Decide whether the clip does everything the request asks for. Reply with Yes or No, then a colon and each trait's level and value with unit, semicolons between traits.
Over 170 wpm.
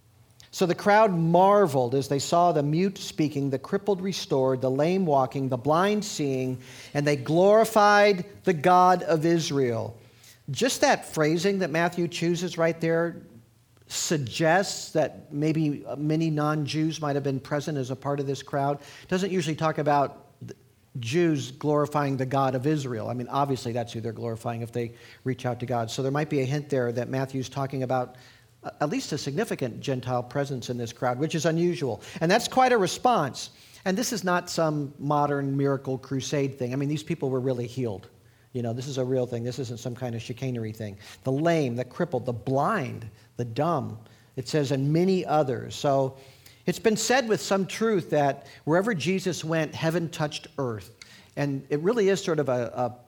Yes: average, 190 wpm